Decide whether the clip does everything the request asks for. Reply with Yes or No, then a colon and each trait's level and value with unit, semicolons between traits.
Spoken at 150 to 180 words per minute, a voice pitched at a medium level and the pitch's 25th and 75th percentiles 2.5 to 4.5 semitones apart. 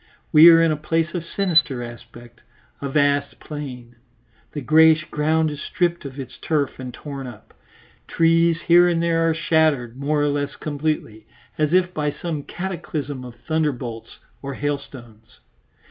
Yes: average, 155 wpm; medium, 150 Hz; average, 3.4 semitones